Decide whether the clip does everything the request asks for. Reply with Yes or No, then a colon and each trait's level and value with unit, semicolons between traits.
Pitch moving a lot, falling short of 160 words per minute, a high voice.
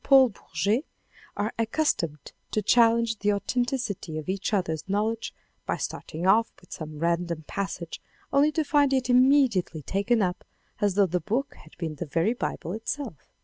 No: wide, 6.0 semitones; average, 165 wpm; high, 205 Hz